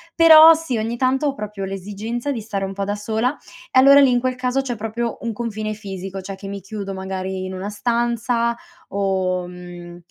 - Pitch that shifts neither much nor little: Yes, average, 4.1 semitones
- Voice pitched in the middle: No, high, 215 Hz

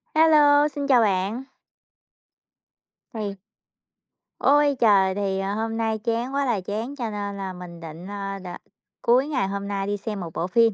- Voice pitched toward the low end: No, high, 210 Hz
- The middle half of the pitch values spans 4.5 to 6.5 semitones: No, average, 4.1 semitones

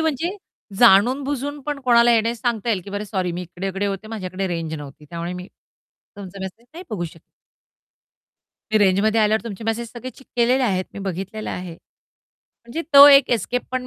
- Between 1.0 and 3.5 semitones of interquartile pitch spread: No, average, 4.8 semitones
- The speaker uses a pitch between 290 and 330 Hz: No, high, 215 Hz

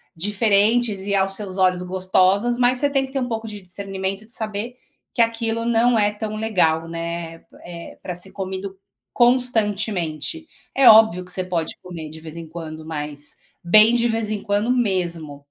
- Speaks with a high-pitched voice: Yes, high, 200 Hz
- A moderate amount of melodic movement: Yes, average, 4.5 semitones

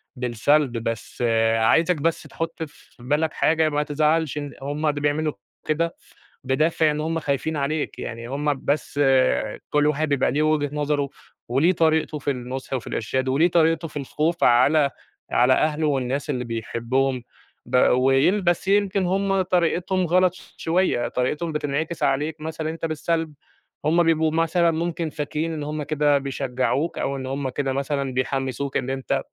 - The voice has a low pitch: No, medium, 150 Hz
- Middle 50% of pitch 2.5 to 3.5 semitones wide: Yes, average, 3.2 semitones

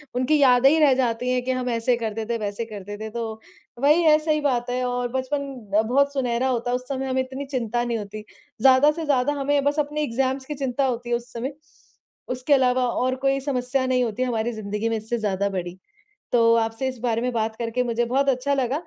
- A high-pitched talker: Yes, very high, 250 Hz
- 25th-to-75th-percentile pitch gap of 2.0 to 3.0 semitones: Yes, average, 2.7 semitones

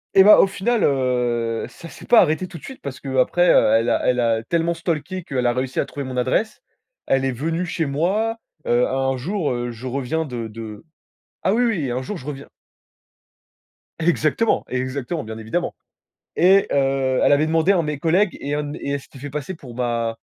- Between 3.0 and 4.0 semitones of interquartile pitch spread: No, average, 5.3 semitones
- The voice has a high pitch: No, medium, 140 Hz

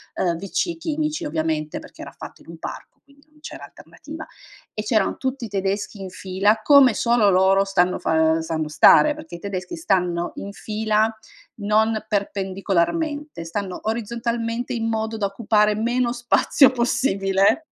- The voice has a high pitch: Yes, high, 215 Hz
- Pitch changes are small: No, average, 3.9 semitones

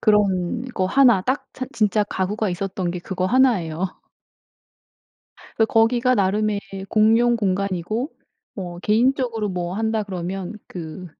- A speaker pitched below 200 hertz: No, high, 205 Hz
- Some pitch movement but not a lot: Yes, average, 3.5 semitones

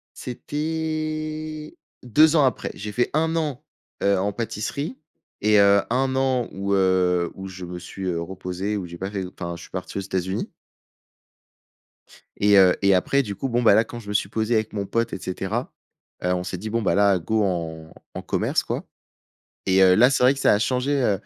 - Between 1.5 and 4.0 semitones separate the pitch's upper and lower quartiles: No, average, 5.2 semitones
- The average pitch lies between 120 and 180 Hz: No, low, 105 Hz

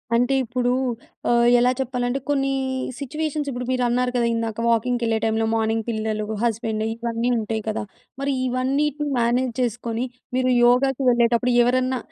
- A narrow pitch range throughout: Yes, narrow, 1.9 semitones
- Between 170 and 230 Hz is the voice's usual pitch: No, high, 245 Hz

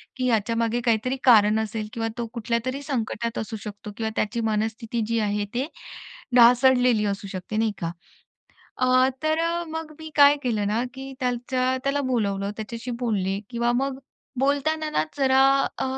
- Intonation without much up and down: No, average, 3.3 semitones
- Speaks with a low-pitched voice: No, high, 235 Hz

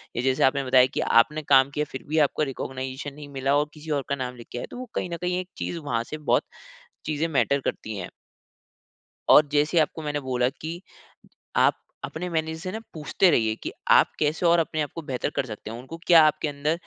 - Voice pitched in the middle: Yes, medium, 145 Hz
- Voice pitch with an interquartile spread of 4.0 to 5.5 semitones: No, average, 3.4 semitones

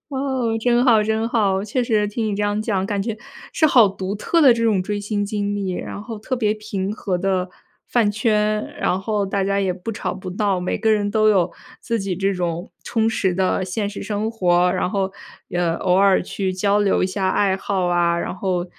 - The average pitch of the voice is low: No, high, 205 Hz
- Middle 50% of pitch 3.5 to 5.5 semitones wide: No, narrow, 2.5 semitones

